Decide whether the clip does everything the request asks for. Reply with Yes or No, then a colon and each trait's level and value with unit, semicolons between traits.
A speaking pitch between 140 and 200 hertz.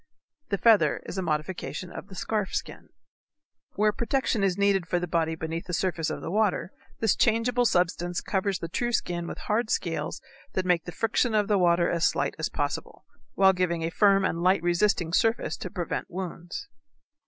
Yes: medium, 185 Hz